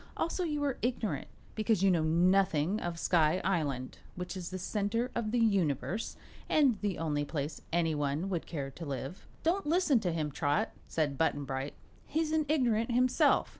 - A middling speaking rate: Yes, average, 170 wpm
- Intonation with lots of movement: Yes, wide, 7.2 semitones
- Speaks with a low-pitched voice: No, medium, 185 Hz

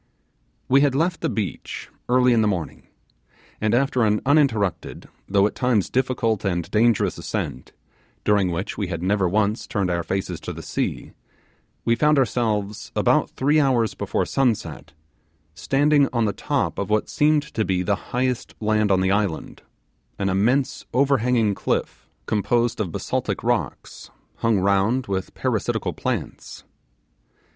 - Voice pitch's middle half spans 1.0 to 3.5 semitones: No, average, 4.4 semitones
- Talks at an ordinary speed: Yes, average, 150 wpm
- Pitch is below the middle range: Yes, low, 110 Hz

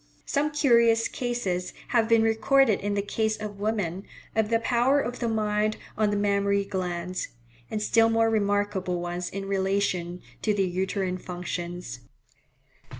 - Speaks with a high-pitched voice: Yes, high, 205 Hz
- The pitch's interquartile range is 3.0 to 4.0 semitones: Yes, average, 3.3 semitones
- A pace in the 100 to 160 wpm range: Yes, average, 150 wpm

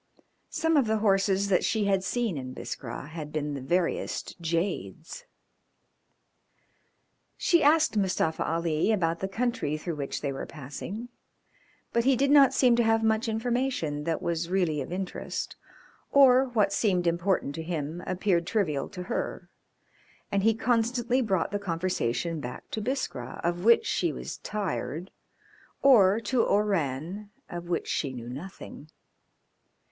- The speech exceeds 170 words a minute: No, average, 145 wpm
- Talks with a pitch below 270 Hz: Yes, high, 190 Hz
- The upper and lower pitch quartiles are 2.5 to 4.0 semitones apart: No, wide, 5.6 semitones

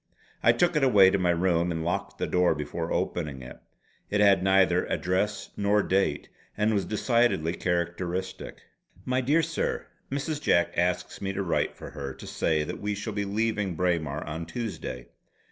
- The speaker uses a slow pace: No, average, 175 wpm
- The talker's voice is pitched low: Yes, very low, 95 Hz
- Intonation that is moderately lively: Yes, average, 3.6 semitones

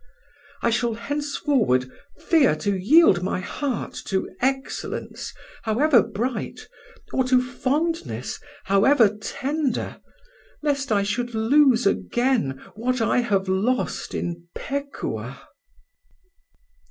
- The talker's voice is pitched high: Yes, high, 245 Hz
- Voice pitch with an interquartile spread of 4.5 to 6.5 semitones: Yes, wide, 5.5 semitones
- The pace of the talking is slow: Yes, slow, 100 wpm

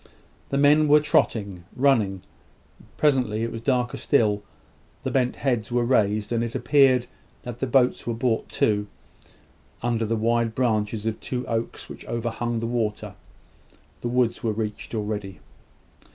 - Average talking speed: Yes, average, 150 wpm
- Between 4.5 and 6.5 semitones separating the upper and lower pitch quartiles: No, narrow, 2.6 semitones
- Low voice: Yes, low, 115 Hz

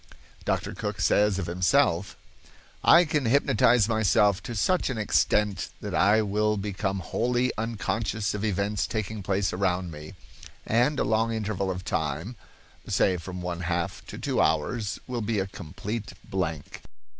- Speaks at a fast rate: No, average, 150 wpm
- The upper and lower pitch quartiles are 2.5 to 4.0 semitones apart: Yes, average, 3.4 semitones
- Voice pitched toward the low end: Yes, low, 105 Hz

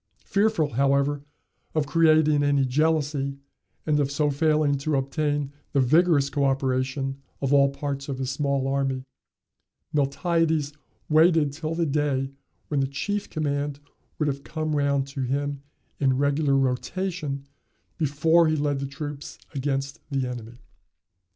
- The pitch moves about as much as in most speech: No, narrow, 2.0 semitones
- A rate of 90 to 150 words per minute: Yes, slow, 135 wpm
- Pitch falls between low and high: Yes, medium, 145 Hz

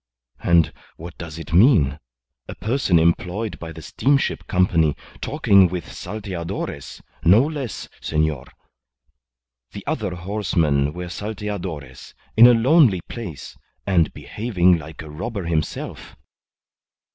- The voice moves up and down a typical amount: Yes, average, 4.8 semitones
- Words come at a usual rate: No, slow, 115 wpm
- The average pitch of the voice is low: Yes, very low, 90 Hz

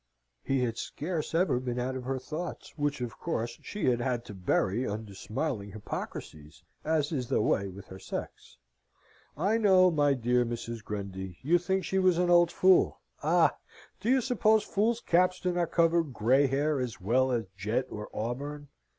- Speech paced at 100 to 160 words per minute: No, average, 180 wpm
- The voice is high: No, low, 130 Hz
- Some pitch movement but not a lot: No, wide, 7.2 semitones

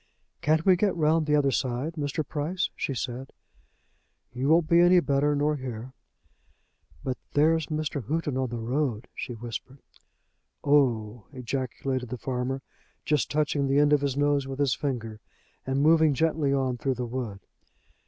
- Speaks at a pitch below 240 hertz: Yes, medium, 140 Hz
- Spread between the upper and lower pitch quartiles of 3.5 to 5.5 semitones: No, average, 3.1 semitones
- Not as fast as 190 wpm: Yes, average, 165 wpm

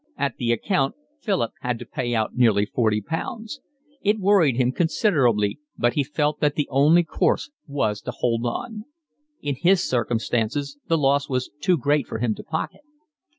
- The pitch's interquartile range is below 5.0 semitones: No, wide, 5.5 semitones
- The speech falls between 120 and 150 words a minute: No, average, 170 wpm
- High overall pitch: No, medium, 140 Hz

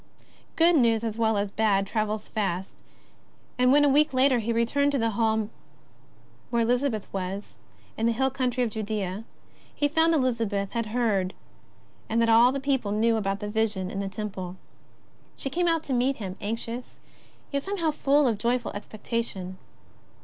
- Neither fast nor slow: Yes, average, 170 wpm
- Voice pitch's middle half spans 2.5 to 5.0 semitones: Yes, average, 4.0 semitones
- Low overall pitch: No, high, 230 Hz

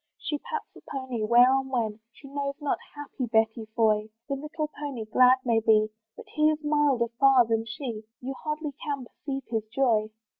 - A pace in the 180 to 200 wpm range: Yes, average, 185 wpm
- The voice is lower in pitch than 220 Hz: No, very high, 255 Hz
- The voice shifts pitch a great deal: No, average, 4.3 semitones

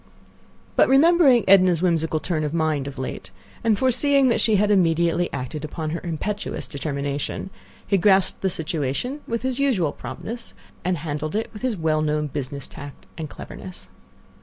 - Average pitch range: No, wide, 6.0 semitones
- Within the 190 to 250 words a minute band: No, average, 160 wpm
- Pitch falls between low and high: Yes, medium, 170 Hz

